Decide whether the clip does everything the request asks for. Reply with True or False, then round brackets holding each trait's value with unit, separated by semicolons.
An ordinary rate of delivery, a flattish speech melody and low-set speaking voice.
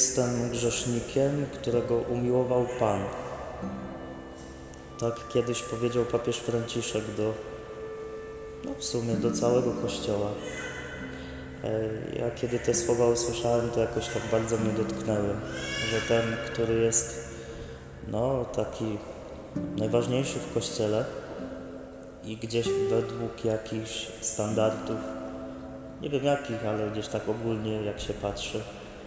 False (105 wpm; 2.0 semitones; 115 Hz)